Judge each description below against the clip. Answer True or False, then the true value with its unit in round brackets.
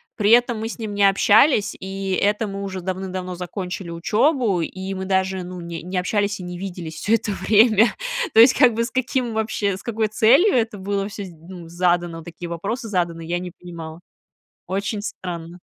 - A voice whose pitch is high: True (195 Hz)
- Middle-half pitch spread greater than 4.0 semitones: False (3.5 semitones)